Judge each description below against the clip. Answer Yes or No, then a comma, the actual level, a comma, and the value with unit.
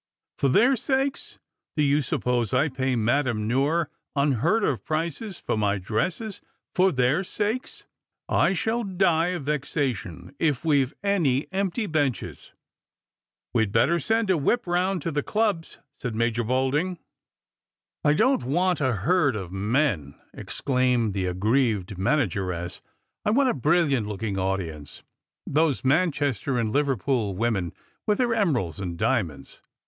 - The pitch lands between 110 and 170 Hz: Yes, medium, 140 Hz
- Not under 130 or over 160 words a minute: Yes, average, 150 wpm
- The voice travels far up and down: Yes, wide, 7.8 semitones